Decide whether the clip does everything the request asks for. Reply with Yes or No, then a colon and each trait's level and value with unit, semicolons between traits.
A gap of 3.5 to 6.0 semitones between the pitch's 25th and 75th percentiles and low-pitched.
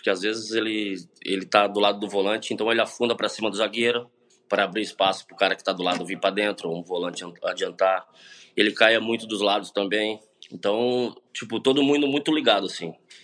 No: average, 2.7 semitones; low, 105 Hz